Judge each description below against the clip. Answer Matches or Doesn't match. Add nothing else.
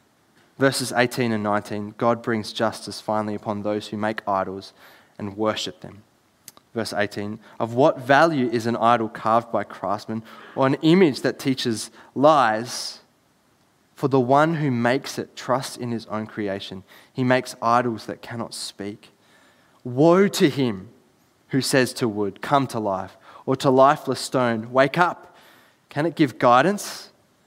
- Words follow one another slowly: Doesn't match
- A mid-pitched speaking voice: Doesn't match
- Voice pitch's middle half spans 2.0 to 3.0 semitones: Doesn't match